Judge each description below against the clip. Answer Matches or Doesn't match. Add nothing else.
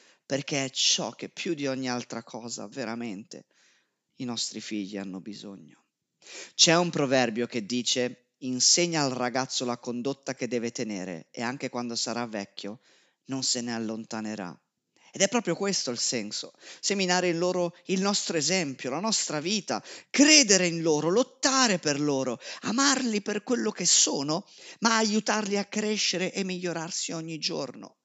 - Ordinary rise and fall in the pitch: Doesn't match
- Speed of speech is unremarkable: Matches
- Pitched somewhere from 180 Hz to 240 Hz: Doesn't match